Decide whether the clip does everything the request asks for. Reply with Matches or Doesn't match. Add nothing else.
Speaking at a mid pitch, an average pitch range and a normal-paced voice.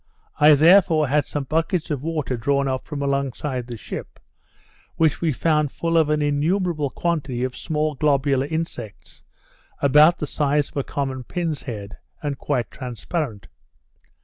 Matches